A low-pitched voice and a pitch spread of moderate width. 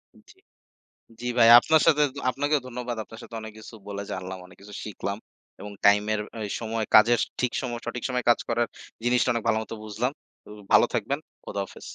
Yes: low, 115 Hz; average, 3.0 semitones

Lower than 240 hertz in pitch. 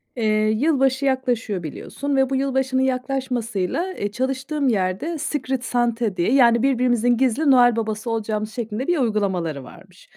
No: high, 245 Hz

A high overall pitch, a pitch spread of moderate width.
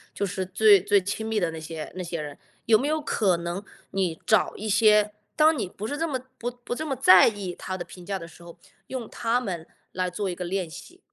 Yes: high, 195 Hz; average, 4.4 semitones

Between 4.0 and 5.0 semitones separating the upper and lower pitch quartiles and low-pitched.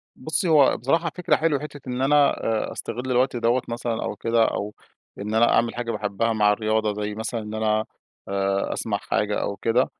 No: average, 3.3 semitones; low, 115 Hz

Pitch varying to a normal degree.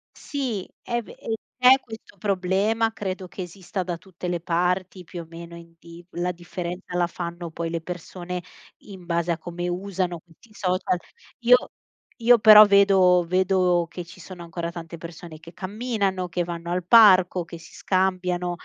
No: narrow, 2.0 semitones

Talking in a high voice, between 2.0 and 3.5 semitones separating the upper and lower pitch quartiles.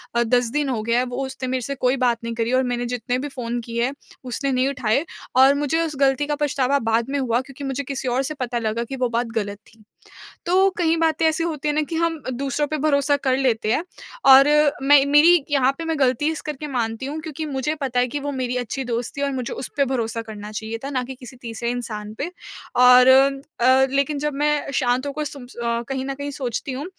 Yes: very high, 265 Hz; average, 2.9 semitones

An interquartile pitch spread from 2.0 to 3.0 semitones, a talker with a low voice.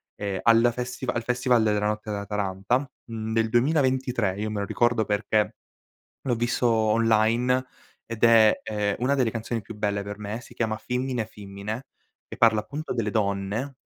Yes: average, 2.7 semitones; low, 110 Hz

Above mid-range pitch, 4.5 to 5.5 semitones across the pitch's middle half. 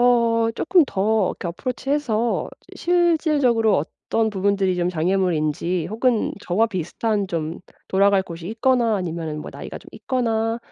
Yes: high, 215 Hz; average, 4.8 semitones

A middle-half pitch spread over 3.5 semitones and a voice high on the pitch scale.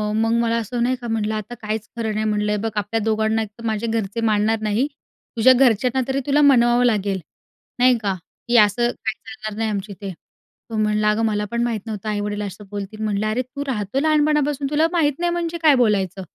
No: average, 3.0 semitones; high, 225 Hz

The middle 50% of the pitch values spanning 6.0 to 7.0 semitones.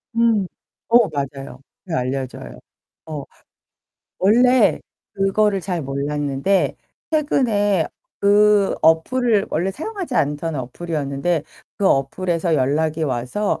Yes: wide, 6.5 semitones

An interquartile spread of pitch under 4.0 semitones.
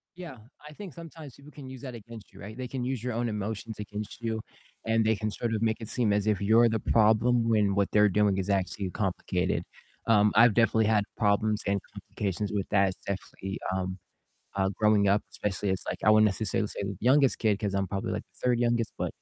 Yes: average, 2.8 semitones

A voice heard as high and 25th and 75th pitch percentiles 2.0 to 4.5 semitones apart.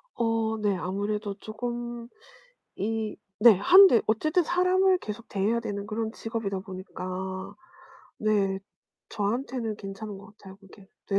Yes: high, 215 Hz; average, 2.9 semitones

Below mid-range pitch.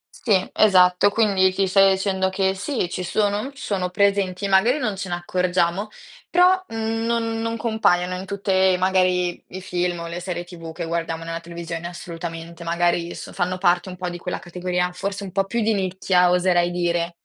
No: medium, 185 Hz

